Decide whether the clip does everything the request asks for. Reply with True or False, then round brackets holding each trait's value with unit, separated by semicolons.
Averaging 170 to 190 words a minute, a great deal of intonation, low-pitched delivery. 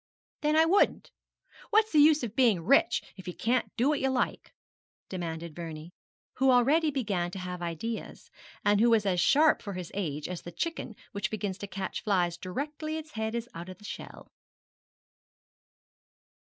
False (175 wpm; 7.0 semitones; 210 Hz)